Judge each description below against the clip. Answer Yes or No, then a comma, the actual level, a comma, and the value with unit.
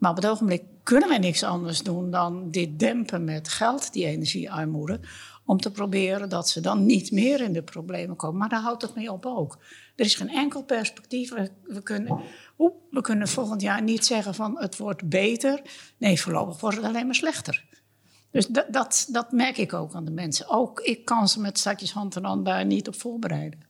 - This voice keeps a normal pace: No, fast, 210 wpm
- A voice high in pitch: Yes, high, 205 Hz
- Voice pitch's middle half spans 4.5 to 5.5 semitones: Yes, average, 4.9 semitones